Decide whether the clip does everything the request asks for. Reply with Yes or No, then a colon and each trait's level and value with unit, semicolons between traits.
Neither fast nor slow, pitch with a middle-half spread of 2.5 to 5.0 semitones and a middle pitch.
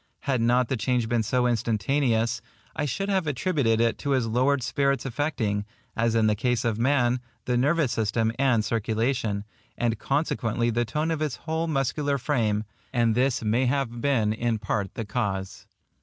No: average, 170 wpm; average, 3.5 semitones; low, 120 Hz